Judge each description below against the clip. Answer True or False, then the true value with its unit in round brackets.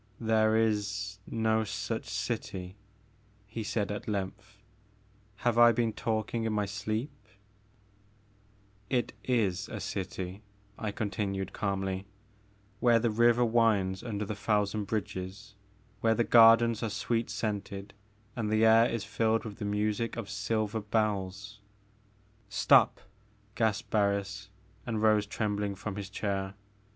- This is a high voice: False (105 Hz)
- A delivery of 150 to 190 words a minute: False (135 wpm)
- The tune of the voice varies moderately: False (1.8 semitones)